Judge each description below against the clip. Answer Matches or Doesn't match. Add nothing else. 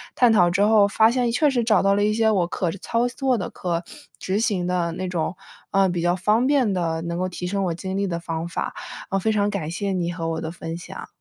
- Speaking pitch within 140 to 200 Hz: Matches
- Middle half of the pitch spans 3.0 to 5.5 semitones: Matches